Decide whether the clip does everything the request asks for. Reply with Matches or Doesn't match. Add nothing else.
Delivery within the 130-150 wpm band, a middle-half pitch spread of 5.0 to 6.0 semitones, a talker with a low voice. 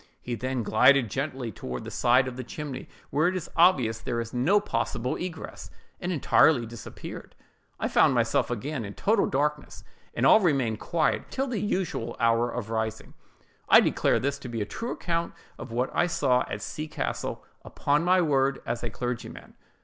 Doesn't match